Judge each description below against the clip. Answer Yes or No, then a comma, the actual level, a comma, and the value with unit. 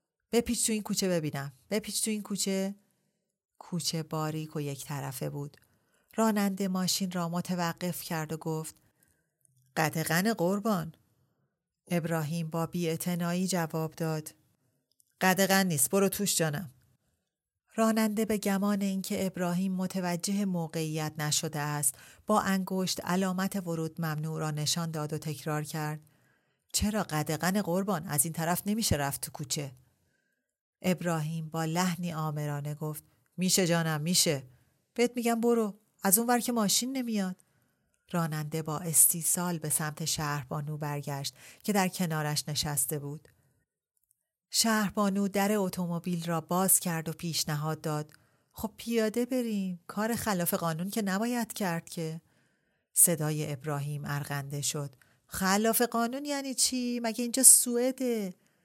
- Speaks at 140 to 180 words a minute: No, average, 125 wpm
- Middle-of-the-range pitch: Yes, medium, 170 Hz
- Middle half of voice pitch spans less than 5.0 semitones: Yes, average, 4.5 semitones